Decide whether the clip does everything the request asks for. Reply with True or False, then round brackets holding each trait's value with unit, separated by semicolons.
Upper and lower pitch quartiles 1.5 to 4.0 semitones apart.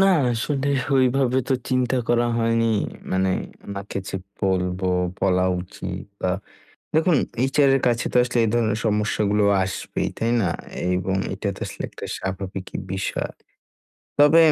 False (5.0 semitones)